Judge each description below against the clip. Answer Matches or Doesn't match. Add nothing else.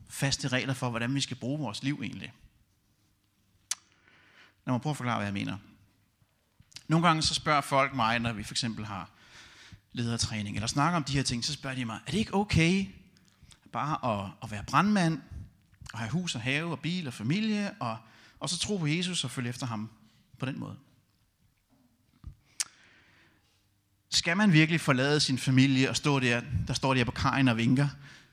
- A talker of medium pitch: Doesn't match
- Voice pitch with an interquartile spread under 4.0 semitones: Doesn't match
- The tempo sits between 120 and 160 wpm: Doesn't match